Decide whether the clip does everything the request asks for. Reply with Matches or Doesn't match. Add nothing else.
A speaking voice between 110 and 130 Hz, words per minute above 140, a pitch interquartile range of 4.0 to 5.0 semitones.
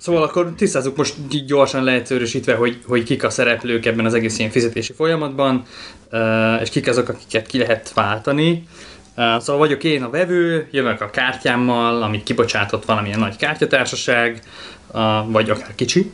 Matches